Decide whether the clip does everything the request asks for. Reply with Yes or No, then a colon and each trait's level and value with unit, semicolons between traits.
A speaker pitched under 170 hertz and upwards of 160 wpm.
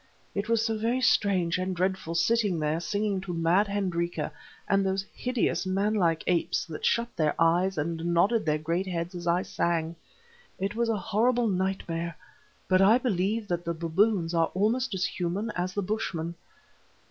No: medium, 185 Hz; average, 170 wpm